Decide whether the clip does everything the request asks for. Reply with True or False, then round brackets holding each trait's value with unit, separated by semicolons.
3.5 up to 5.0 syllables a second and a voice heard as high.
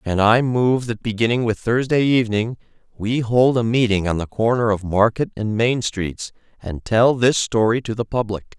False (4.8 syllables/s; 115 Hz)